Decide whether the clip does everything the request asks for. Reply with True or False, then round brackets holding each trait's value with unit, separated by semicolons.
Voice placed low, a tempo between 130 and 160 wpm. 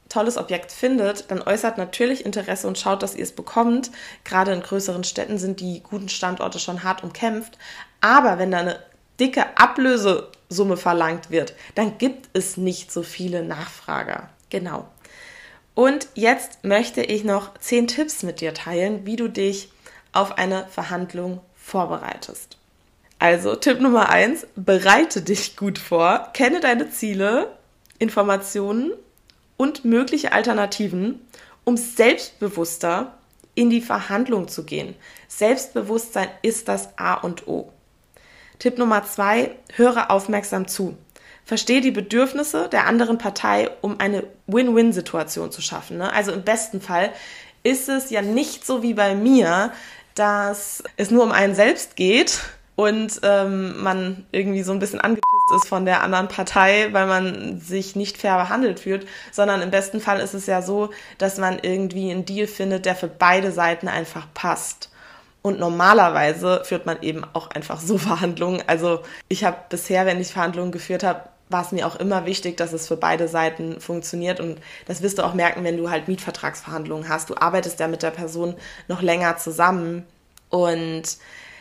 False (195 Hz; 155 wpm)